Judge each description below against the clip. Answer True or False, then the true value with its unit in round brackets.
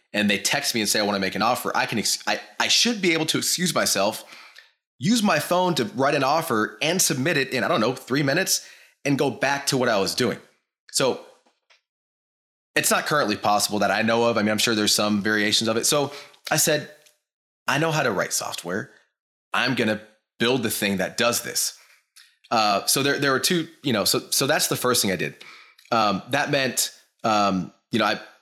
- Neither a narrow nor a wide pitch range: False (5.9 semitones)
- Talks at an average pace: False (225 wpm)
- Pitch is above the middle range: False (125 Hz)